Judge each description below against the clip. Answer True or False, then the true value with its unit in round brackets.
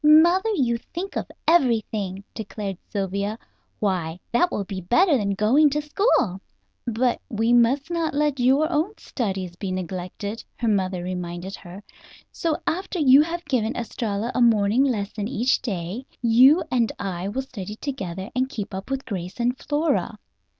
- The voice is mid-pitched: False (230 Hz)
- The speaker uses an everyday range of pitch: False (6.0 semitones)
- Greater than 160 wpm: False (155 wpm)